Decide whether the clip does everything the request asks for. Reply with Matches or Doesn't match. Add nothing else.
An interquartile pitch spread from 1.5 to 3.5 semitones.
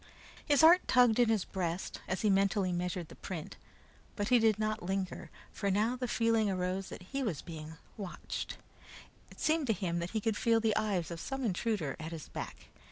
Doesn't match